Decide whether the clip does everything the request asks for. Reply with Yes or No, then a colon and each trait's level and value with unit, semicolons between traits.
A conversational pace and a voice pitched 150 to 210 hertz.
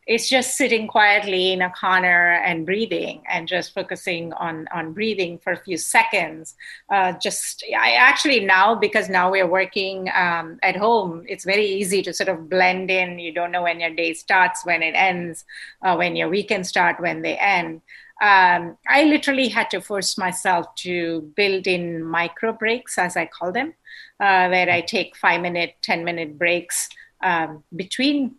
Yes: average, 180 wpm; medium, 185 Hz